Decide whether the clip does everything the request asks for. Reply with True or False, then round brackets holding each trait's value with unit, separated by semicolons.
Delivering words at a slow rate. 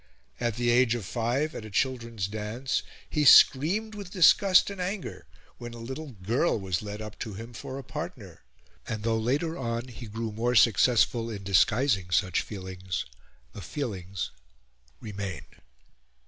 False (155 wpm)